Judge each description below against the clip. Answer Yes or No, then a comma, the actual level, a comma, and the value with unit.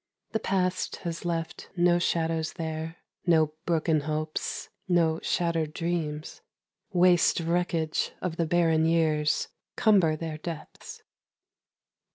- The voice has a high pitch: No, medium, 165 Hz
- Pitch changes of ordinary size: No, narrow, 1.7 semitones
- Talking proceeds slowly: Yes, slow, 110 wpm